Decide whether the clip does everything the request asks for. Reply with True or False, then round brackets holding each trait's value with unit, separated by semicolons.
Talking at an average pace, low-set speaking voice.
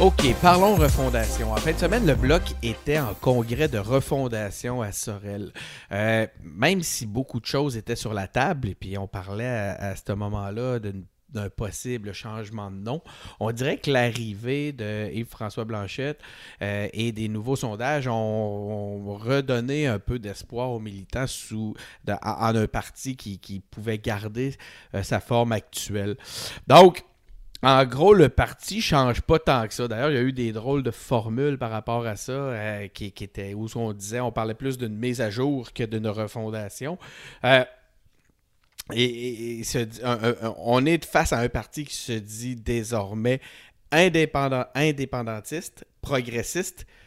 True (175 wpm; 115 Hz)